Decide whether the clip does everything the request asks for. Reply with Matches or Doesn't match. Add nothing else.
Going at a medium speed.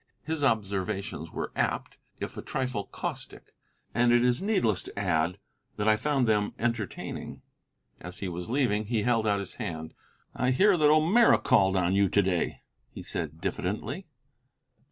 Matches